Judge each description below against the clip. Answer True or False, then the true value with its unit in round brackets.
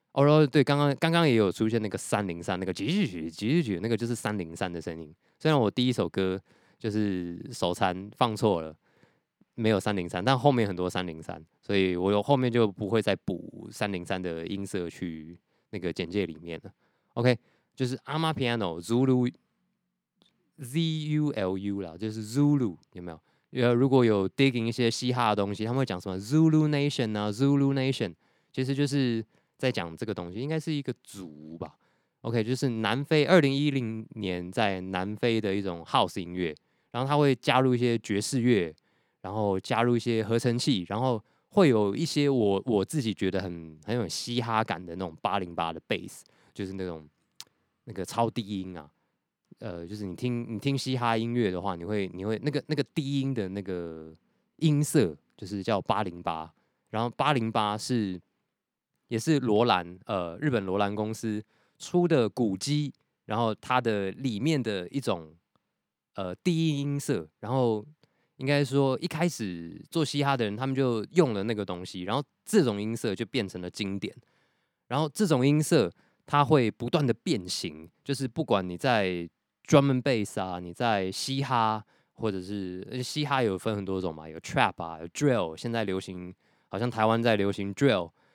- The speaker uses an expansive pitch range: True (5.9 semitones)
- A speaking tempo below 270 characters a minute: False (295 characters per minute)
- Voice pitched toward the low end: True (110 Hz)